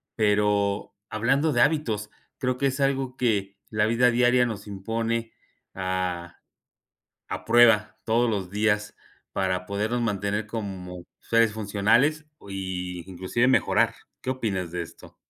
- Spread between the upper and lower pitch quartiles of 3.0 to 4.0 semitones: Yes, average, 3.6 semitones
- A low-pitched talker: Yes, low, 105 Hz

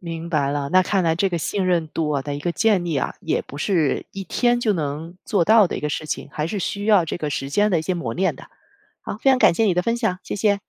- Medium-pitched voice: Yes, medium, 175 Hz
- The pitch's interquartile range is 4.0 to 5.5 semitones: Yes, average, 4.8 semitones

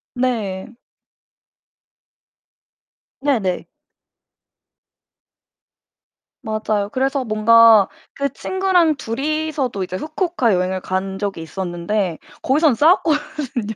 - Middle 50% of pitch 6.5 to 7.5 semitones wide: Yes, wide, 7.0 semitones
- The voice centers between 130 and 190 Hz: No, high, 230 Hz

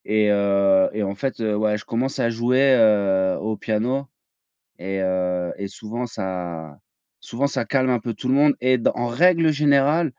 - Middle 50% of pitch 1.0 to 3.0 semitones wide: No, average, 4.9 semitones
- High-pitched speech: No, low, 110 Hz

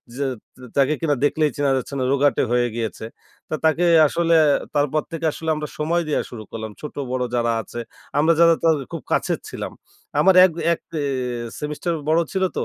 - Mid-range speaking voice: Yes, medium, 150 Hz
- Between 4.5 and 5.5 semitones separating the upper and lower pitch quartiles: No, average, 4.1 semitones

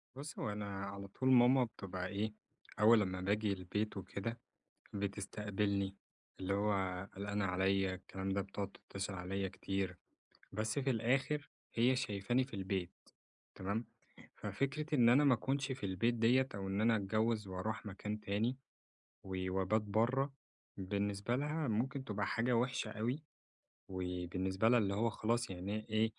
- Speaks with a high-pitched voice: No, low, 105 Hz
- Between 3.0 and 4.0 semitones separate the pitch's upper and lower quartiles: Yes, average, 3.5 semitones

